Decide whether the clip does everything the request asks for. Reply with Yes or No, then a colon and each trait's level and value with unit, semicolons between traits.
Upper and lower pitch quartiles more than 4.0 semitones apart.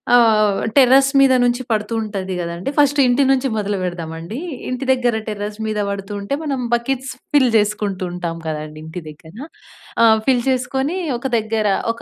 Yes: average, 5.0 semitones